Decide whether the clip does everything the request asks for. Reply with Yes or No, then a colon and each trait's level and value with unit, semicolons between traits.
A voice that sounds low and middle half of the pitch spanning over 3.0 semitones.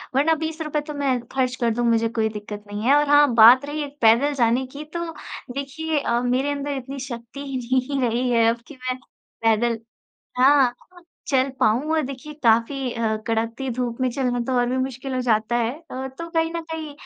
No: very high, 255 Hz; average, 3.5 semitones